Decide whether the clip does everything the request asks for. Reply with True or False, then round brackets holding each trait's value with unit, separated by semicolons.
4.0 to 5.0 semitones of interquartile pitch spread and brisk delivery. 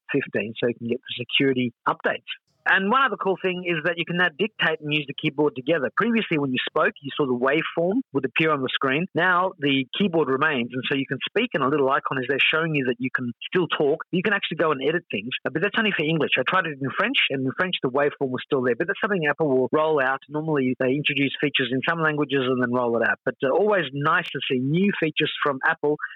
True (4.6 semitones; 255 wpm)